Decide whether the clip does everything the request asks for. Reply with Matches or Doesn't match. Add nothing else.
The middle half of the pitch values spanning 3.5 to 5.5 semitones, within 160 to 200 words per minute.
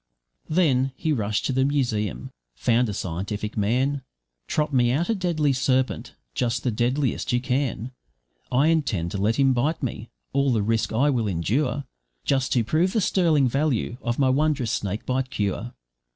Matches